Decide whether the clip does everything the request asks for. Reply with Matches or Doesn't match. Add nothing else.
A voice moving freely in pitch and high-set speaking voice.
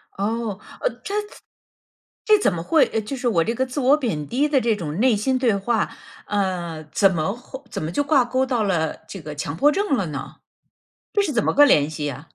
Matches